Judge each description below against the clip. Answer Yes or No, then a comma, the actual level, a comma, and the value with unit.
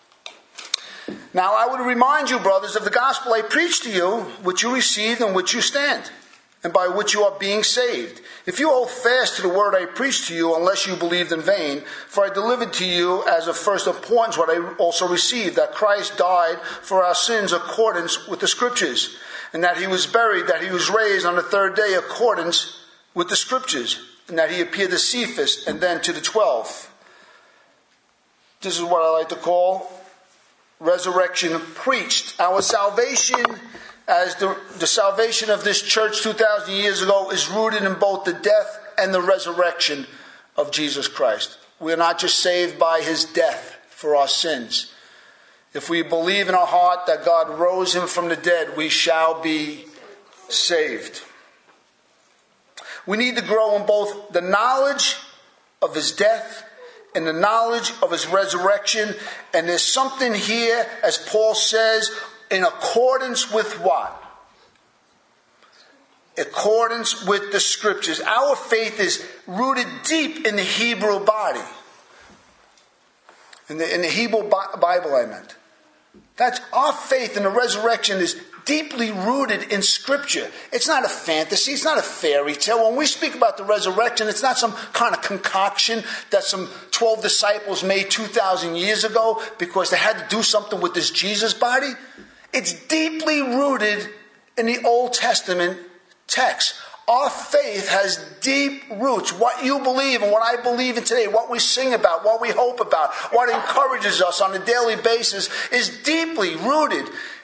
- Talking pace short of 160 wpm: No, average, 165 wpm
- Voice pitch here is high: Yes, high, 210 Hz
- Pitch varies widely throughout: No, average, 4.8 semitones